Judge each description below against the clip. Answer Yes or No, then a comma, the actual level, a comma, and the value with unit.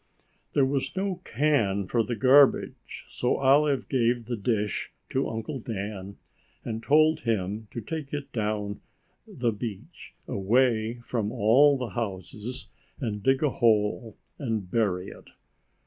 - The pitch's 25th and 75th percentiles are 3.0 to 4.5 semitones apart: Yes, average, 4.2 semitones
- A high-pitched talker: No, low, 115 Hz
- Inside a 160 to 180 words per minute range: No, slow, 135 wpm